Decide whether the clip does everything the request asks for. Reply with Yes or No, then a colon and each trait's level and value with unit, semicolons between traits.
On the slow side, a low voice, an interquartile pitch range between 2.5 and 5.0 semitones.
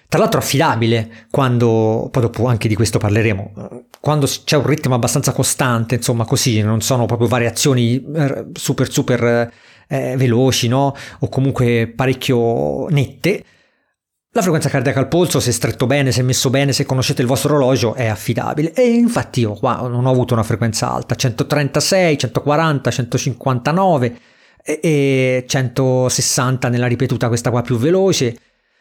No: average, 145 wpm; low, 130 Hz; average, 2.8 semitones